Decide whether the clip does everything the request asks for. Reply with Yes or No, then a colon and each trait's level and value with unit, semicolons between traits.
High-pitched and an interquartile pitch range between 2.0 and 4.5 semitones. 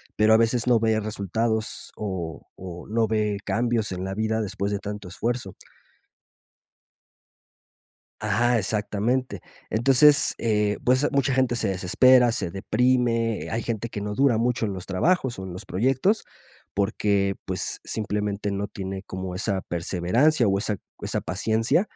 No: low, 110 Hz; average, 3.4 semitones